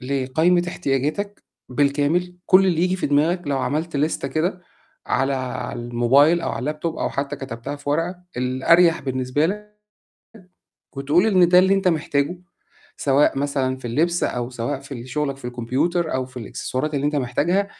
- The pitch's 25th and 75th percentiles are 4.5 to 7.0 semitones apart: Yes, average, 4.8 semitones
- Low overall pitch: No, medium, 145 Hz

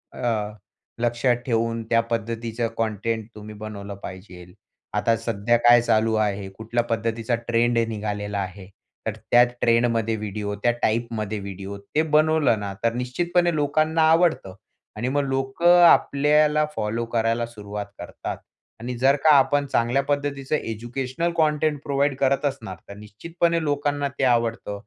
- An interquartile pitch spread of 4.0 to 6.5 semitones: Yes, average, 4.7 semitones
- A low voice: Yes, low, 120 Hz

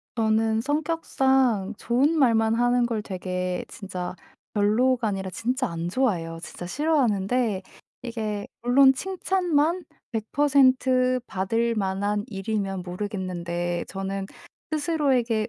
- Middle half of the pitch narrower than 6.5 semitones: Yes, average, 5.2 semitones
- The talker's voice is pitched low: No, high, 225 Hz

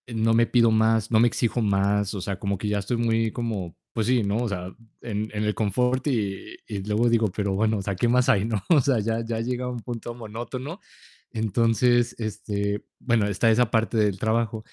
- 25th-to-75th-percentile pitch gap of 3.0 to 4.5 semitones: No, narrow, 2.5 semitones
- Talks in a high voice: No, low, 110 Hz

